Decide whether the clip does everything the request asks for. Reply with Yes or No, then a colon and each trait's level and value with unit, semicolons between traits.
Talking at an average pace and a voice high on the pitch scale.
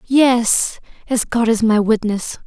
Yes: average, 145 wpm; high, 230 Hz